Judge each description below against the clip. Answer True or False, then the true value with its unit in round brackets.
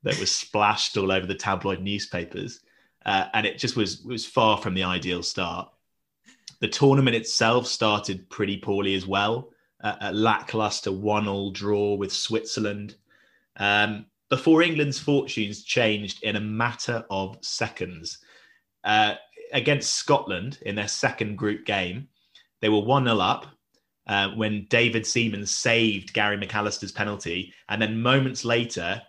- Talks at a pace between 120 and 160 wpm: True (140 wpm)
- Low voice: True (105 Hz)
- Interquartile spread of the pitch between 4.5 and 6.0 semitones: False (2.6 semitones)